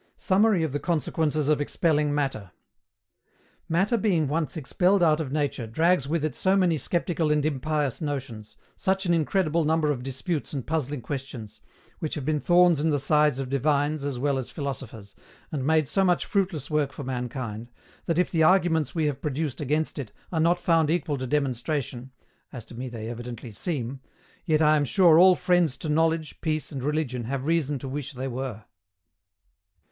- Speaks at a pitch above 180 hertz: No, medium, 150 Hz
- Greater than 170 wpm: Yes, average, 185 wpm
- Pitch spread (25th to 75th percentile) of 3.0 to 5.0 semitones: Yes, average, 3.6 semitones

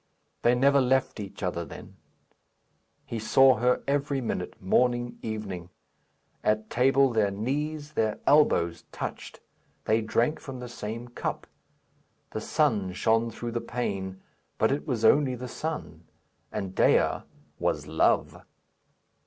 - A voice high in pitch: No, low, 120 Hz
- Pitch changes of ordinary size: Yes, average, 3.8 semitones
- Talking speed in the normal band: No, slow, 130 wpm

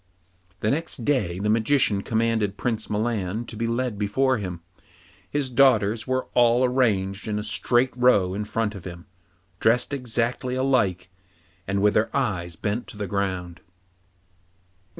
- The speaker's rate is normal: Yes, average, 150 wpm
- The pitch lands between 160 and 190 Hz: No, low, 110 Hz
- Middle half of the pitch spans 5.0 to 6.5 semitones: No, average, 3.8 semitones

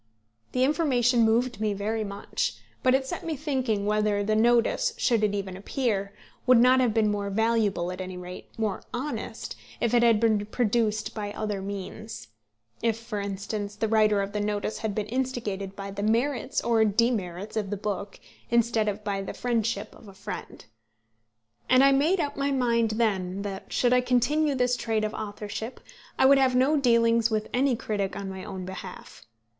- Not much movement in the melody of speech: No, average, 3.3 semitones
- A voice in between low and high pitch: No, high, 220 Hz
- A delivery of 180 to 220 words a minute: Yes, average, 185 wpm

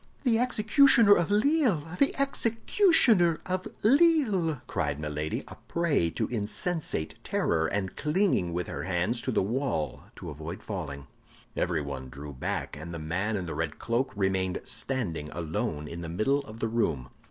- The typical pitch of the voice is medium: No, low, 110 Hz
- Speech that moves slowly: No, average, 155 wpm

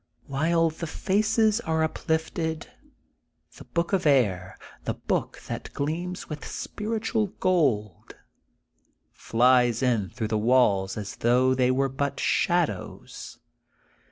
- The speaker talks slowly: Yes, slow, 125 wpm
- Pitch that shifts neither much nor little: No, wide, 5.9 semitones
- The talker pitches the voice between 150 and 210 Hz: No, medium, 140 Hz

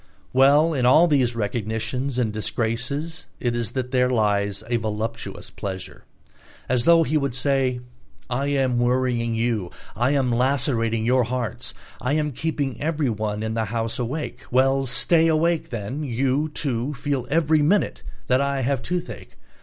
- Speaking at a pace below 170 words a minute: Yes, average, 155 wpm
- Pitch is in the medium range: No, low, 125 Hz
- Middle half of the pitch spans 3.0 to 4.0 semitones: Yes, average, 3.6 semitones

